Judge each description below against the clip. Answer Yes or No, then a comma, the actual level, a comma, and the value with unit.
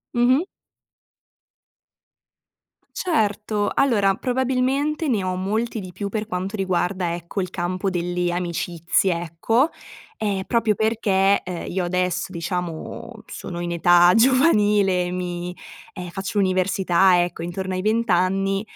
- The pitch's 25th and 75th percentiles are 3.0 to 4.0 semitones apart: Yes, average, 3.4 semitones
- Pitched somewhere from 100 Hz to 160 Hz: No, high, 190 Hz